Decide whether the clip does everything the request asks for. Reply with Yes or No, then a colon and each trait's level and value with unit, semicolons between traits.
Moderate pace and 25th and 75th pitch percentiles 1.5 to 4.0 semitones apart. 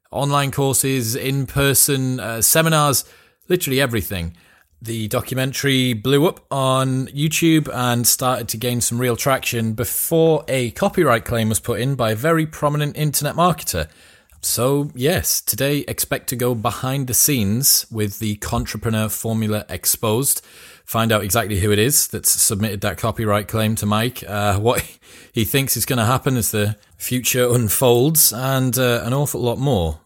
Yes: average, 155 wpm; average, 3.6 semitones